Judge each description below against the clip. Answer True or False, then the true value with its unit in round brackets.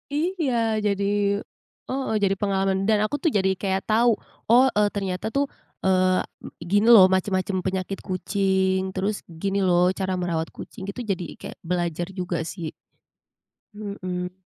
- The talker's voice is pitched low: False (190 Hz)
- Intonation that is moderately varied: False (2.0 semitones)